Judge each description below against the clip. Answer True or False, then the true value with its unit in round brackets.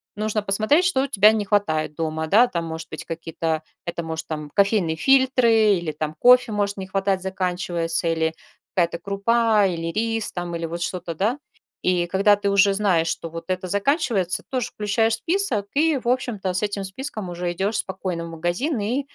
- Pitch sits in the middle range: False (195 Hz)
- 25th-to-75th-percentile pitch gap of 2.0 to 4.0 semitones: False (4.6 semitones)